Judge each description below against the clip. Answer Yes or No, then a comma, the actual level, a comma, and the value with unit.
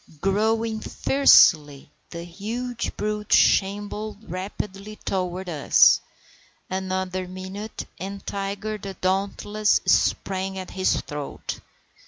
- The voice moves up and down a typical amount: No, narrow, 2.2 semitones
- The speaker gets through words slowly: Yes, slow, 95 wpm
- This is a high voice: Yes, high, 195 Hz